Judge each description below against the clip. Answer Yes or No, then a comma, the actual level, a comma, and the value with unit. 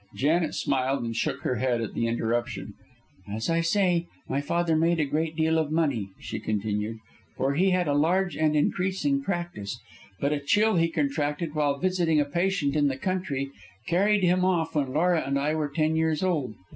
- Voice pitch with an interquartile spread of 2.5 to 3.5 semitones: No, average, 4.0 semitones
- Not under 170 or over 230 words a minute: Yes, average, 190 wpm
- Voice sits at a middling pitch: Yes, medium, 155 Hz